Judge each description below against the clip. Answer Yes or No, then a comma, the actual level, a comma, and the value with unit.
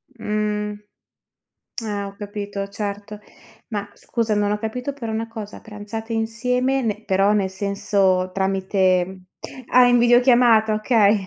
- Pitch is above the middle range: Yes, high, 210 Hz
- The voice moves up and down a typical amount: No, narrow, 2.2 semitones